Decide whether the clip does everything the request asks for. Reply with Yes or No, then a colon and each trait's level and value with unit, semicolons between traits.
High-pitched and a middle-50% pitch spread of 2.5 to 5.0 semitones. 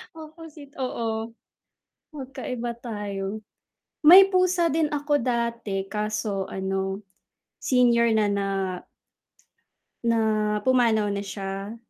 No: high, 235 Hz; wide, 5.5 semitones